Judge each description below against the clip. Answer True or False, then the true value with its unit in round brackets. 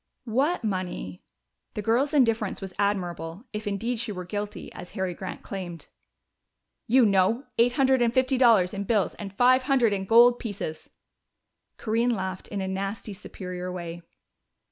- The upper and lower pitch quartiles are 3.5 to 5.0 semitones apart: True (4.2 semitones)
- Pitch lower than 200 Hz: False (205 Hz)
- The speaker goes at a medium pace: True (155 wpm)